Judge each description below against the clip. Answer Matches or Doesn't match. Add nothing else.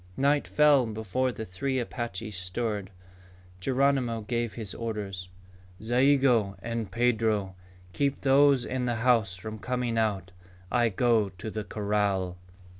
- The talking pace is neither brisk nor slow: Doesn't match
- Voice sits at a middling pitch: Doesn't match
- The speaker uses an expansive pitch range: Doesn't match